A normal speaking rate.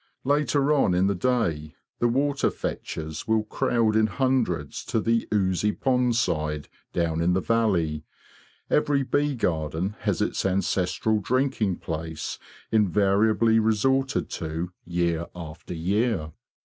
No: slow, 125 wpm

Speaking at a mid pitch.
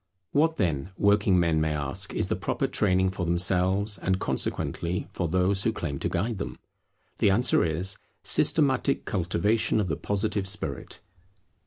No: very low, 95 Hz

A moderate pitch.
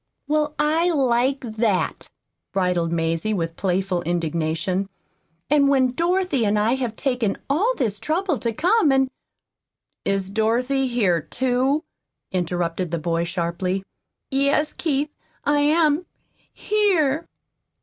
No: high, 245 Hz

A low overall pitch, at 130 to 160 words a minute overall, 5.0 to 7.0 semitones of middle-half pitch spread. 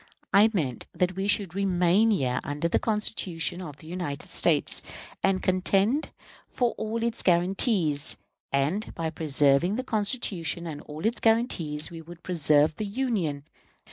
No: medium, 180 Hz; average, 145 wpm; average, 5.3 semitones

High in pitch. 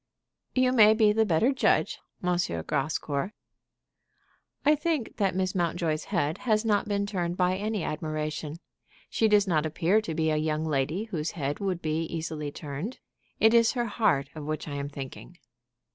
No: medium, 175 Hz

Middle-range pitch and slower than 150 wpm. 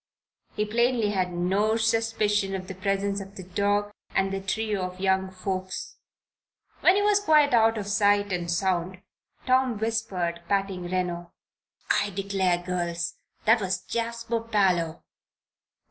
No: high, 195 Hz; average, 140 wpm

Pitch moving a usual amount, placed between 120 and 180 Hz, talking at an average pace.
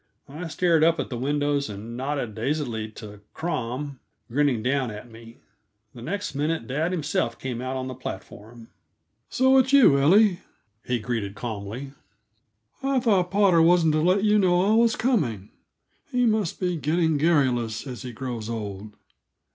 No: wide, 7.1 semitones; medium, 140 Hz; average, 160 wpm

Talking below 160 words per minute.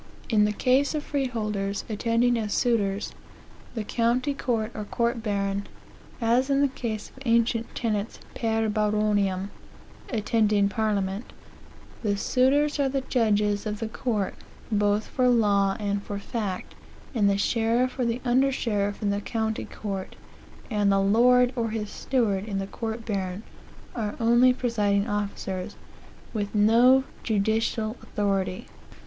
Yes: average, 140 wpm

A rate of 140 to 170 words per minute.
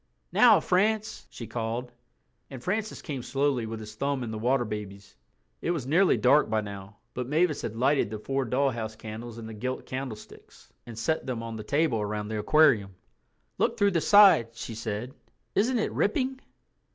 No: average, 180 wpm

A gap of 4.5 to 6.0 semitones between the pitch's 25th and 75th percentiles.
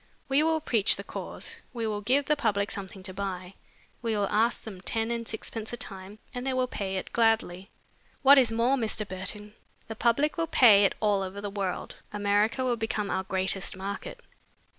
No: average, 3.4 semitones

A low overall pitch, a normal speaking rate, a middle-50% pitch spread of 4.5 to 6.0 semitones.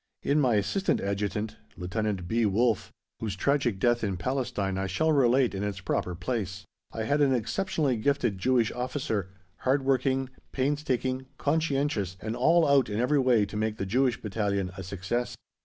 Yes: low, 120 Hz; average, 160 wpm; average, 5.0 semitones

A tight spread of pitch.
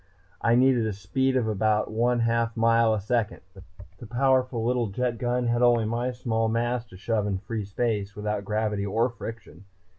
Yes: narrow, 2.3 semitones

